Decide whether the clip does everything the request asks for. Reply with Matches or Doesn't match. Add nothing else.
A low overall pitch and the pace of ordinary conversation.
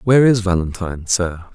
Matches